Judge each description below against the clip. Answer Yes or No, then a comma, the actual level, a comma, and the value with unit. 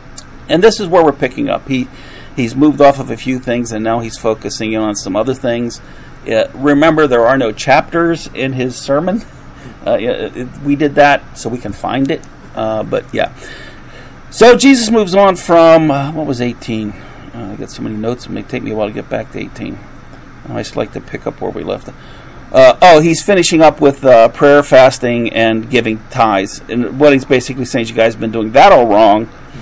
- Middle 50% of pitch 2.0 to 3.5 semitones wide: No, average, 4.7 semitones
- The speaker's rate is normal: No, fast, 215 wpm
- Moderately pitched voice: No, low, 130 Hz